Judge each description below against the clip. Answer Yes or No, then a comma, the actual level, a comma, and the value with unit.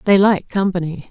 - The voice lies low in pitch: No, high, 190 Hz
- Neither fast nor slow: Yes, average, 165 wpm